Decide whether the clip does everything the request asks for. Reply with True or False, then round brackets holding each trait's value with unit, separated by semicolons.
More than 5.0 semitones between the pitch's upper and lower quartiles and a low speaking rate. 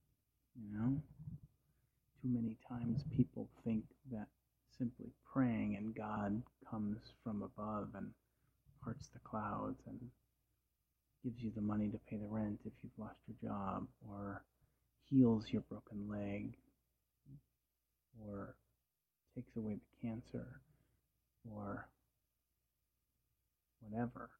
False (3.1 semitones; 110 wpm)